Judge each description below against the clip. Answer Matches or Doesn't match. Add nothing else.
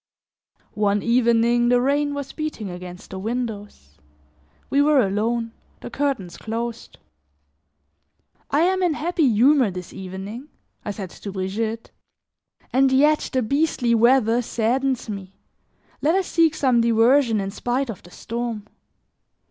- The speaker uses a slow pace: Matches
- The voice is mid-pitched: Doesn't match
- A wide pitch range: Doesn't match